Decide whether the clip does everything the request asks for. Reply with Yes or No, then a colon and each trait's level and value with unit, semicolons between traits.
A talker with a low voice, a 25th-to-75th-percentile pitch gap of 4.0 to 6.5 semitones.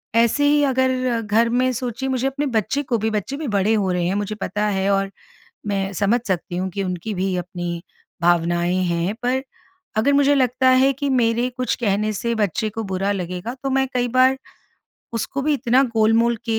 No: high, 225 Hz; average, 4.9 semitones